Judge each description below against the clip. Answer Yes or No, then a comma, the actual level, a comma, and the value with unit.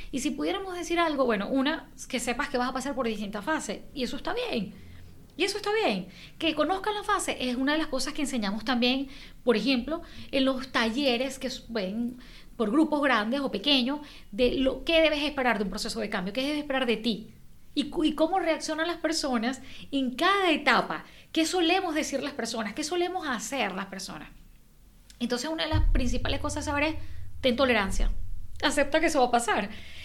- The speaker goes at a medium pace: No, fast, 200 wpm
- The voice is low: No, very high, 270 Hz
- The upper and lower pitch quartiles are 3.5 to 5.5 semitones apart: Yes, average, 4.2 semitones